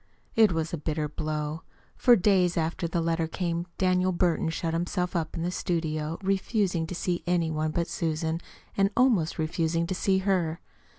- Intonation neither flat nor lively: No, narrow, 2.2 semitones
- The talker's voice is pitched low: No, medium, 170 Hz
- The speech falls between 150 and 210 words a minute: Yes, average, 175 wpm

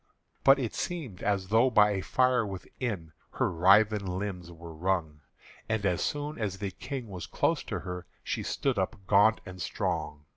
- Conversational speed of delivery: Yes, average, 175 wpm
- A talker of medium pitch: No, low, 100 Hz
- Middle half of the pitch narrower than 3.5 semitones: No, average, 3.8 semitones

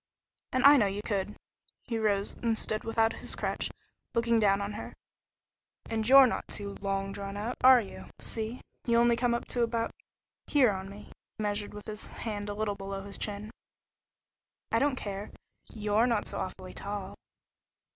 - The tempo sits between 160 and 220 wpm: Yes, average, 175 wpm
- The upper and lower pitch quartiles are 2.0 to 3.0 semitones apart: Yes, narrow, 2.5 semitones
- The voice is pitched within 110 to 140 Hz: No, high, 210 Hz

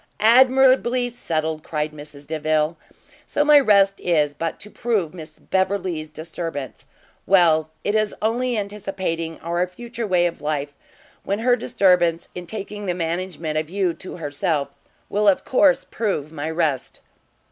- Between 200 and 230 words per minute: No, average, 145 wpm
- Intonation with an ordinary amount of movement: Yes, average, 4.9 semitones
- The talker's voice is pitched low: No, medium, 175 Hz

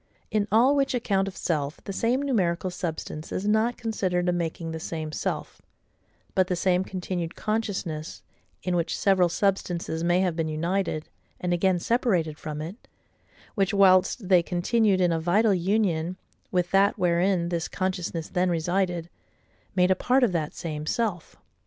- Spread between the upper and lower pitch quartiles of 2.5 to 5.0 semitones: Yes, average, 2.8 semitones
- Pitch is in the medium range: Yes, medium, 180 Hz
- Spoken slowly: No, average, 160 wpm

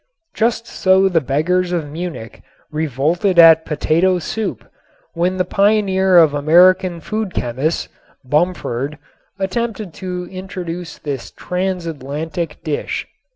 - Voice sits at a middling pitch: Yes, medium, 175 Hz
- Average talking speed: No, slow, 110 wpm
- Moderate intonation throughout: Yes, average, 3.4 semitones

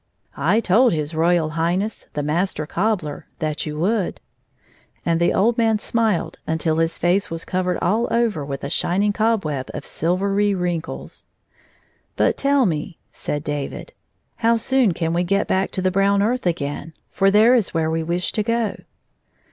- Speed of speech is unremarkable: Yes, average, 180 wpm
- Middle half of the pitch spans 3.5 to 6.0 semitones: Yes, average, 4.8 semitones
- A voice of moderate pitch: Yes, medium, 180 Hz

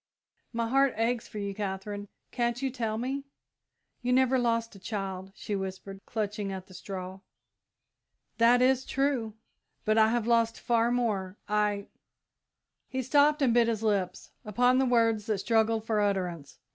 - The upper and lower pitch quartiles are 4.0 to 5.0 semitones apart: No, average, 3.3 semitones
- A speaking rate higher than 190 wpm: No, average, 160 wpm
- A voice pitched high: Yes, high, 225 Hz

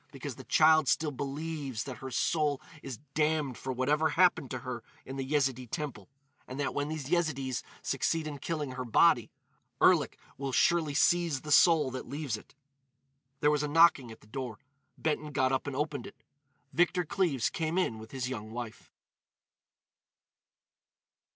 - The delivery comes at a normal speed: Yes, average, 165 wpm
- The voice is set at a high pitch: No, medium, 140 Hz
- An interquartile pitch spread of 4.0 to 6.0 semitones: No, average, 3.4 semitones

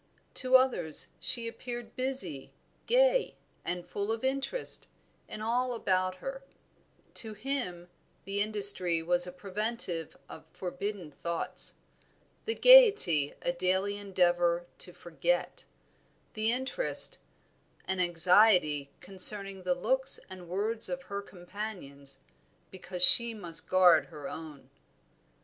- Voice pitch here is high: Yes, high, 195 Hz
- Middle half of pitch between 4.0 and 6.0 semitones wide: Yes, average, 5.1 semitones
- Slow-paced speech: Yes, slow, 115 wpm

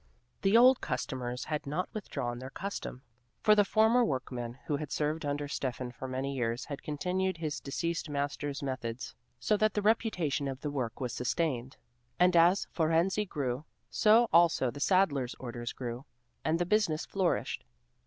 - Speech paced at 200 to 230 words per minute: No, average, 165 wpm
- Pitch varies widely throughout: Yes, wide, 6.0 semitones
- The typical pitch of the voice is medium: Yes, medium, 145 Hz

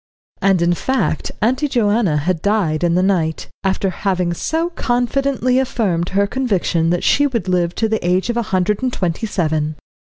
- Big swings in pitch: Yes, wide, 5.8 semitones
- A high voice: Yes, high, 195 Hz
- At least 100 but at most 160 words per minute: No, average, 175 wpm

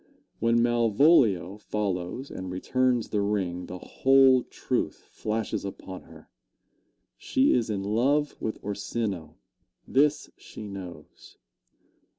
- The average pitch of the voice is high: No, low, 105 Hz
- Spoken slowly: Yes, slow, 110 wpm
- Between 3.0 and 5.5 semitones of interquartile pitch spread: Yes, average, 4.8 semitones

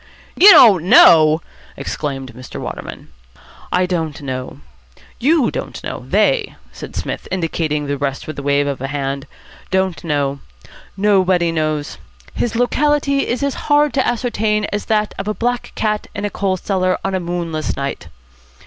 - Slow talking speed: No, average, 155 wpm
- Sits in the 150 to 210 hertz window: Yes, medium, 185 Hz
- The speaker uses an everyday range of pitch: No, wide, 6.9 semitones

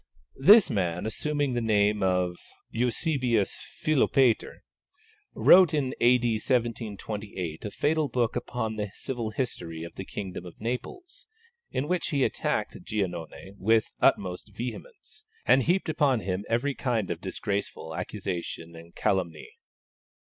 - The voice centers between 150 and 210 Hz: No, low, 110 Hz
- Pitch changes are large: Yes, wide, 5.8 semitones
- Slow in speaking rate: Yes, slow, 130 wpm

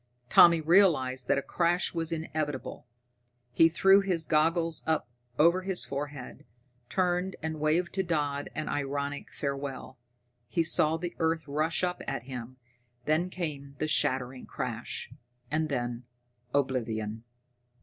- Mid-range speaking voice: Yes, medium, 155 Hz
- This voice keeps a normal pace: No, slow, 130 wpm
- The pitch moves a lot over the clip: No, average, 3.5 semitones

